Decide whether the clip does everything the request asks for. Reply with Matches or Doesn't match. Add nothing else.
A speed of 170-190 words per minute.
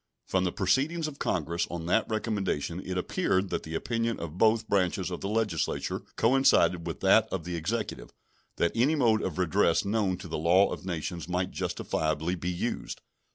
Matches